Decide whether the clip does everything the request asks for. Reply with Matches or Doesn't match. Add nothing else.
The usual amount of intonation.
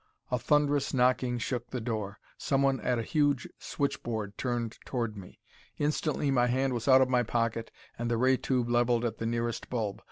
Doesn't match